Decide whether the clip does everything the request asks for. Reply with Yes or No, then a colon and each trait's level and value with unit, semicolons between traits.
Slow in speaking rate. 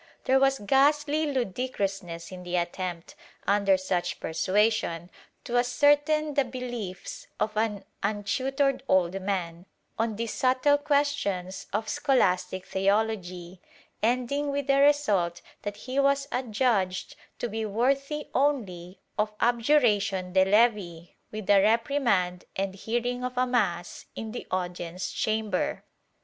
Yes: slow, 125 wpm